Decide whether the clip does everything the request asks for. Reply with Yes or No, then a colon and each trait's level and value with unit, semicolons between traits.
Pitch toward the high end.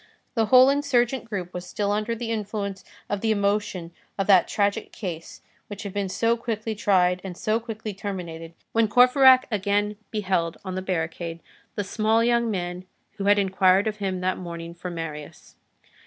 Yes: high, 200 Hz